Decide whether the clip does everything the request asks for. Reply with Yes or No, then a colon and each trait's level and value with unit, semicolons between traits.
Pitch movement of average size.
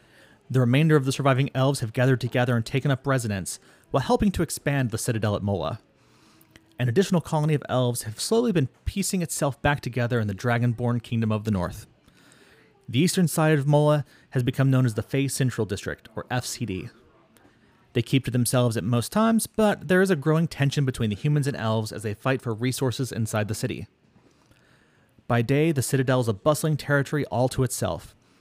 Yes: average, 3.9 semitones